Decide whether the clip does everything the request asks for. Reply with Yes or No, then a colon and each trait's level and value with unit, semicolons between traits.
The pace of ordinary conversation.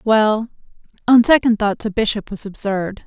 Yes: average, 155 wpm